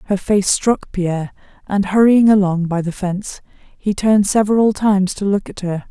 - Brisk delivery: No, average, 185 wpm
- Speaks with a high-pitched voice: Yes, high, 200 Hz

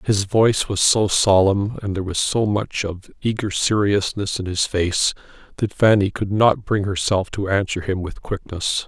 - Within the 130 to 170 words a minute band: No, average, 185 wpm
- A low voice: Yes, low, 100 Hz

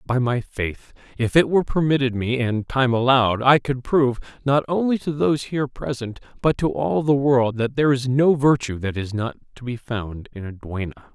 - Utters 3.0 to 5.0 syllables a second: No, 5.2 syllables/s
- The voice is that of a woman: No, male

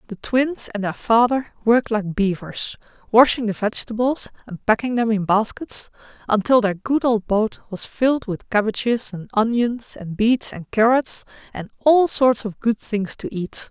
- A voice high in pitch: Yes, high, 225 Hz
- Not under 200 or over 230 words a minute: No, average, 170 wpm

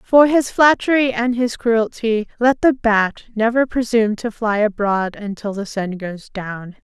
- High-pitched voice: Yes, high, 225 Hz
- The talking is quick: No, average, 185 wpm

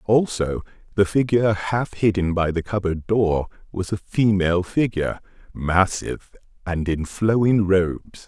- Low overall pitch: Yes, very low, 95 Hz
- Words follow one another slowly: Yes, slow, 125 wpm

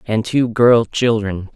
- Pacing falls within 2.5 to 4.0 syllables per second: Yes, 3.5 syllables/s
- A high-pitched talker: No, low, 115 Hz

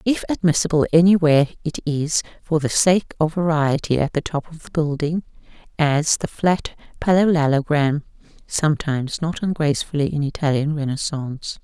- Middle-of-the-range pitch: Yes, medium, 155 Hz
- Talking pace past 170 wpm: No, slow, 135 wpm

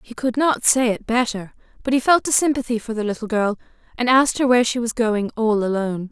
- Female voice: Yes, female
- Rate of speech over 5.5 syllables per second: Yes, 6.0 syllables/s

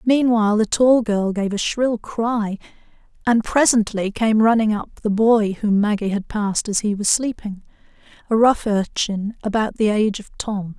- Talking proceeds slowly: No, average, 165 wpm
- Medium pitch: No, high, 215 Hz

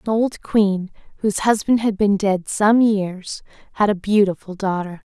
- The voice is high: Yes, high, 205 Hz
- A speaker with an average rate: Yes, average, 165 wpm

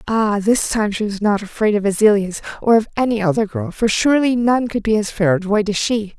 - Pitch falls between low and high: No, high, 215 Hz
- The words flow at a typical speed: No, fast, 245 wpm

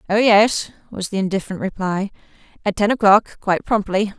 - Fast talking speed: No, average, 160 wpm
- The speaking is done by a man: No, female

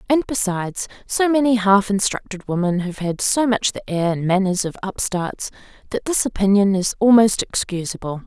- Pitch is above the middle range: Yes, high, 205 Hz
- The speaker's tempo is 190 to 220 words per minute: No, average, 165 wpm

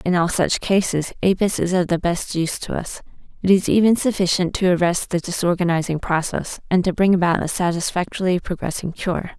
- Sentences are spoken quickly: No, average, 185 wpm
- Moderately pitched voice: Yes, medium, 180 Hz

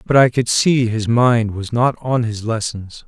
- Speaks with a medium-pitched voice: No, low, 115 Hz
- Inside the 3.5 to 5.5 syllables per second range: Yes, 4.1 syllables/s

